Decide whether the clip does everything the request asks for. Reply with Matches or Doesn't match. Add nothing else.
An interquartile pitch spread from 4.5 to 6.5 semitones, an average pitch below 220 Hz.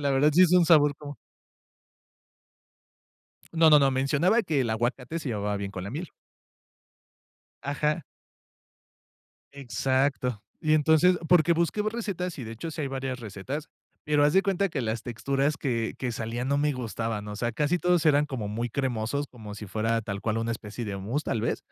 Matches